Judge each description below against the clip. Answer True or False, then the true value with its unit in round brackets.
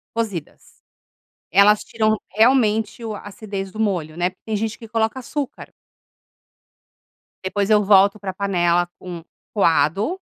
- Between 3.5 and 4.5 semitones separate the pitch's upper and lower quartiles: False (2.8 semitones)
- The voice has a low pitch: False (205 Hz)